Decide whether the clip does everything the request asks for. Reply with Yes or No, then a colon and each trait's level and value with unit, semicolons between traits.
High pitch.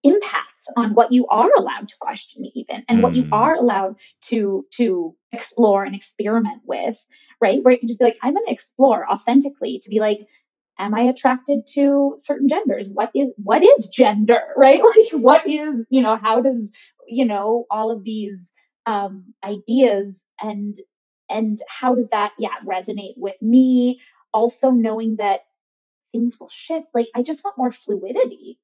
Yes: high, 235 Hz